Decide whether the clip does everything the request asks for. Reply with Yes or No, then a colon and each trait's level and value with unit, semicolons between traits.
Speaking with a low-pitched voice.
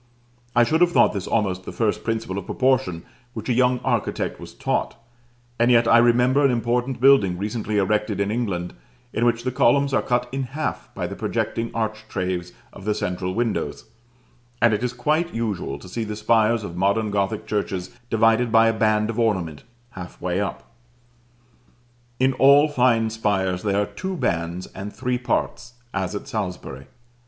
Yes: low, 110 Hz